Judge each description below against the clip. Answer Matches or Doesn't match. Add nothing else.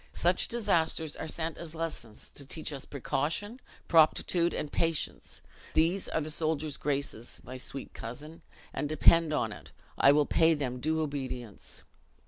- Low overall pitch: Doesn't match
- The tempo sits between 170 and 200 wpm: Doesn't match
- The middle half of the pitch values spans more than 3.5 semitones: Doesn't match